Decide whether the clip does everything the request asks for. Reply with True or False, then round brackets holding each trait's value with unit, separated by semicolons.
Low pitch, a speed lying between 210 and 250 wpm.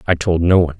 False (85 Hz; 305 wpm)